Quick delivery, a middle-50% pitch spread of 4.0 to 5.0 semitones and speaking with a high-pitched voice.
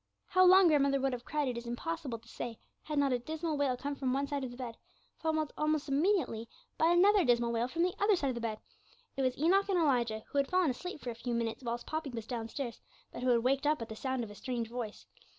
Yes: fast, 255 wpm; average, 4.7 semitones; very high, 270 Hz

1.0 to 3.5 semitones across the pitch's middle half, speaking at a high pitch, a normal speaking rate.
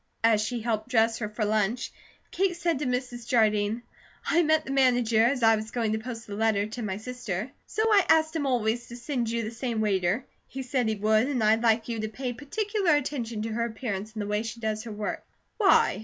No: average, 2.9 semitones; high, 230 Hz; fast, 230 wpm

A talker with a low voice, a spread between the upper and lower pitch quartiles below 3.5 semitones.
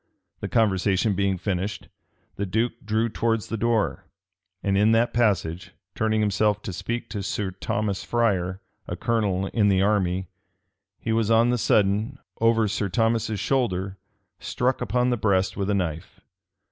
Yes: low, 105 Hz; average, 2.9 semitones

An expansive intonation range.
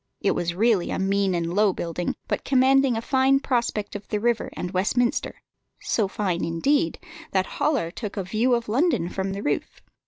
No: average, 4.8 semitones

